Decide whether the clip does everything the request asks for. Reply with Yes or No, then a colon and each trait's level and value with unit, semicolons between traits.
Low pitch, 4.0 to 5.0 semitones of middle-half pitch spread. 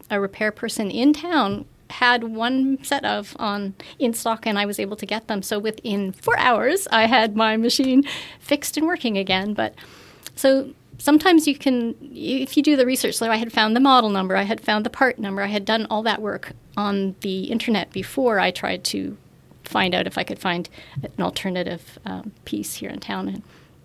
No: high, 225 Hz; average, 4.6 semitones